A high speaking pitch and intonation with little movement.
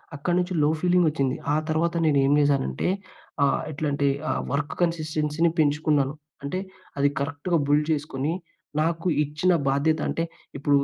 No: medium, 150 Hz; narrow, 2.3 semitones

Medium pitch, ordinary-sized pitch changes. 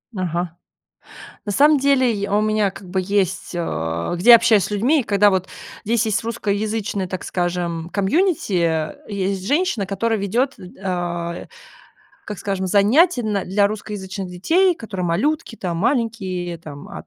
No: high, 200 Hz; average, 4.0 semitones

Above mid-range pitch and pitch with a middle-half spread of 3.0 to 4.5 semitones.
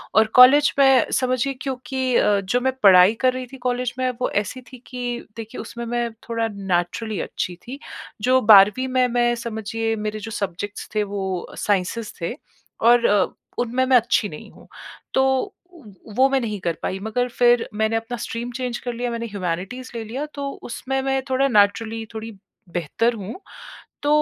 Yes: high, 235 Hz; average, 3.4 semitones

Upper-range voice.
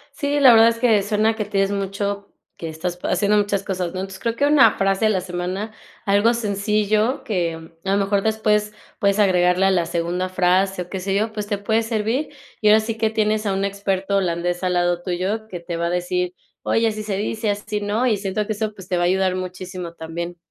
Yes: high, 200 Hz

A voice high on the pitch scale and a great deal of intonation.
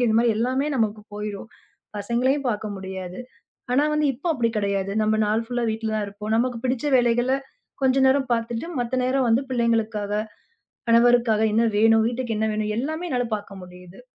No: high, 230 Hz; average, 2.8 semitones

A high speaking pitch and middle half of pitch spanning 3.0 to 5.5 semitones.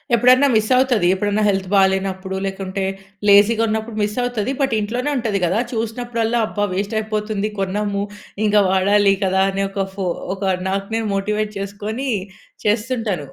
No: high, 210 Hz; narrow, 2.4 semitones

